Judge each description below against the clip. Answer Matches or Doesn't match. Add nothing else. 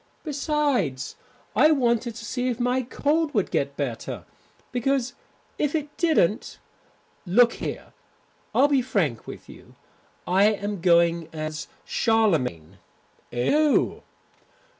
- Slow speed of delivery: Matches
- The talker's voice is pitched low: Doesn't match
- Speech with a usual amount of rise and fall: Doesn't match